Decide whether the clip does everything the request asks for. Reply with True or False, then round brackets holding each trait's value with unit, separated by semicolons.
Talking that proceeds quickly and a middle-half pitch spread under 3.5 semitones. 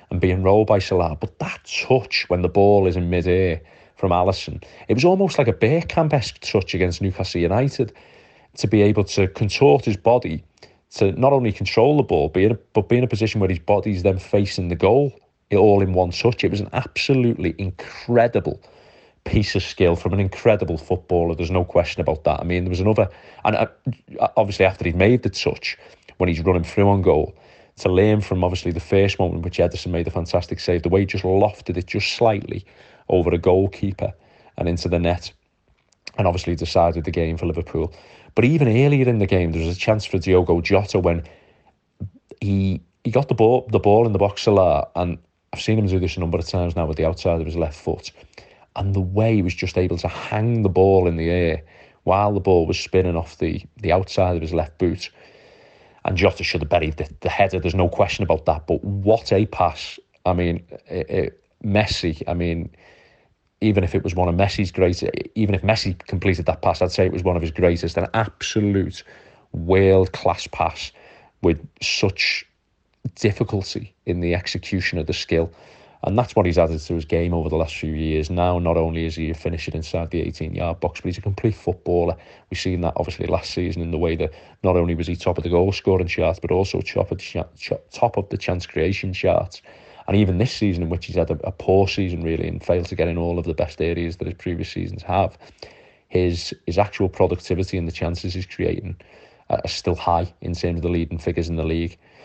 True (215 wpm; 2.8 semitones)